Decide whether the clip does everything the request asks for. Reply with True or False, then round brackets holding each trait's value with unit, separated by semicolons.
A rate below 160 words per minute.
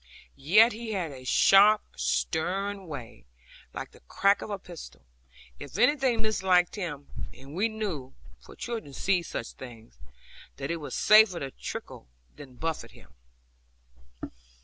True (140 wpm)